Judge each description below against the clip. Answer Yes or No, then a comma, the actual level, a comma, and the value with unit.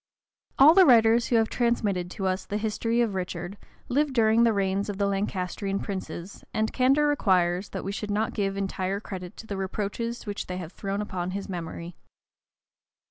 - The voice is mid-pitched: No, high, 200 Hz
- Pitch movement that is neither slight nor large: Yes, average, 3.1 semitones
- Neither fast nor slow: Yes, average, 185 wpm